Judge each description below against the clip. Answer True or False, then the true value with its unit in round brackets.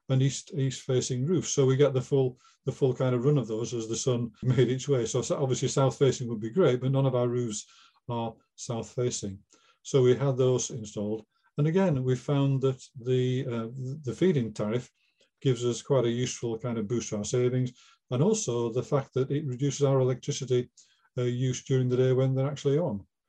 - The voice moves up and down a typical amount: False (1.9 semitones)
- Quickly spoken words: True (210 wpm)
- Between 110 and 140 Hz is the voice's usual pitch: True (130 Hz)